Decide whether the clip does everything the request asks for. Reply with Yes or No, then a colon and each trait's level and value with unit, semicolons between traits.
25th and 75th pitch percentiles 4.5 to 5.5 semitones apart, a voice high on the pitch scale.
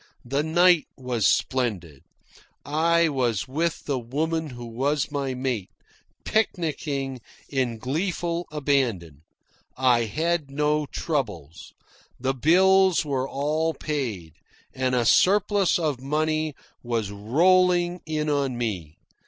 No: average, 4.8 semitones; medium, 140 Hz